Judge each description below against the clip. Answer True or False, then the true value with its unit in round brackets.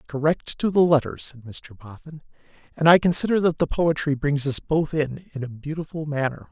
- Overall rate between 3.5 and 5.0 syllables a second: False (5.2 syllables/s)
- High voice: False (145 Hz)